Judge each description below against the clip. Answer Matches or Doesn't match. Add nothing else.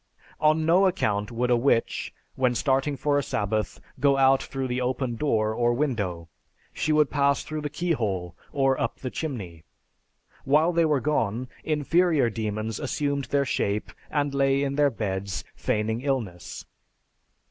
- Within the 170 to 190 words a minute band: Doesn't match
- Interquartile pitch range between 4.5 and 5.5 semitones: Matches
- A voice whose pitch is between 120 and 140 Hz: Matches